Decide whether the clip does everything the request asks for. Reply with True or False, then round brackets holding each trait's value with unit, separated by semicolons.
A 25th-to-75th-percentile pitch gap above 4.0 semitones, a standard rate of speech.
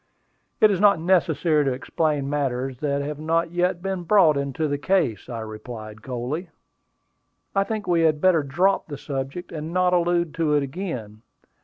True (4.5 semitones; 170 wpm)